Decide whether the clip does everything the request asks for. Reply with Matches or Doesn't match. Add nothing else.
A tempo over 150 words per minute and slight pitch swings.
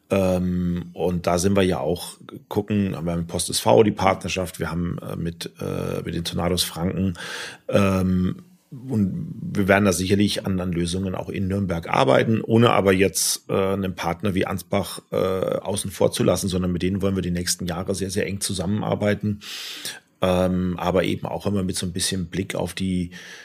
Matches